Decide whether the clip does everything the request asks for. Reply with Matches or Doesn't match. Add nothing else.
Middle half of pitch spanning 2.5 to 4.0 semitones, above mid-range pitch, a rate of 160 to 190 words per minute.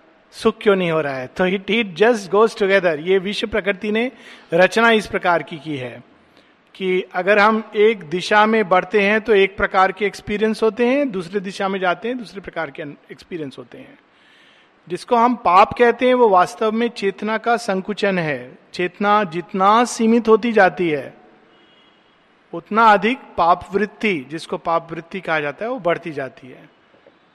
Matches